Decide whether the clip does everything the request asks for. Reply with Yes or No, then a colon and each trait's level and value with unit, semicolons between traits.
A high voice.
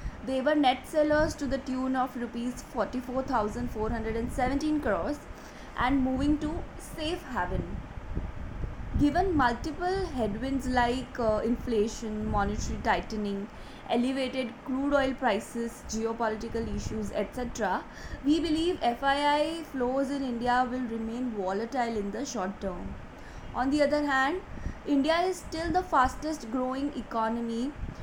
Yes: very high, 255 Hz